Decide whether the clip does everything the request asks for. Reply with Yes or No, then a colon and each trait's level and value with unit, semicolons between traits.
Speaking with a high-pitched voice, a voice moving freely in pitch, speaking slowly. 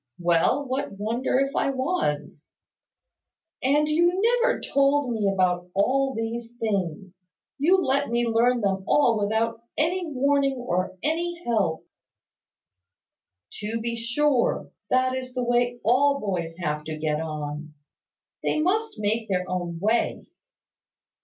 Yes: high, 235 Hz; wide, 6.4 semitones; slow, 130 wpm